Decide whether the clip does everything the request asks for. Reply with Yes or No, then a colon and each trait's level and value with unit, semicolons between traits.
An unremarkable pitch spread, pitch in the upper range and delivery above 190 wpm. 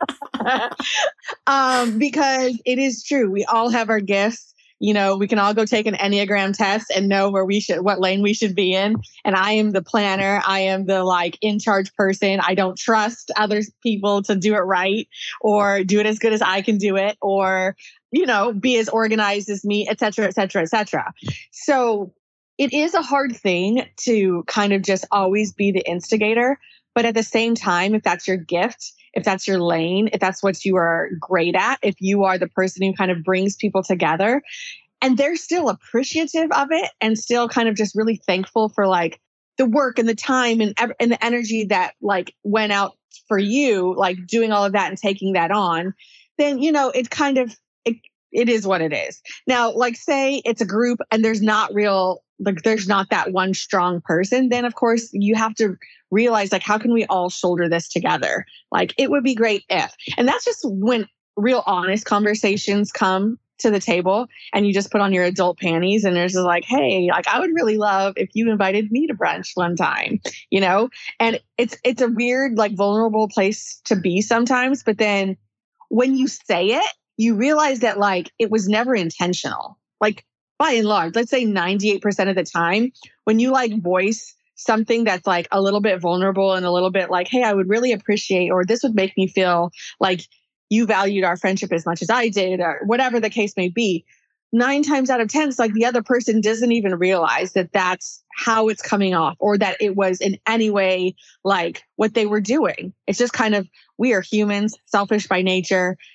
Yes: average, 3.3 semitones; high, 210 Hz; fast, 205 wpm